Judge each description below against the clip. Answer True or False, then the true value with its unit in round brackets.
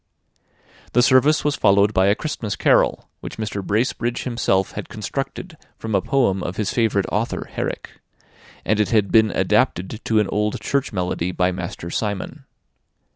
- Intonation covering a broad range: False (3.6 semitones)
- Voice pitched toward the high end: False (105 Hz)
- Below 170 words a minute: True (160 wpm)